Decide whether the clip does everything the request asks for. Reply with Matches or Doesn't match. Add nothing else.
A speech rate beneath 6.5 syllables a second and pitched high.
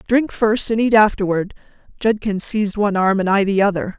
Matches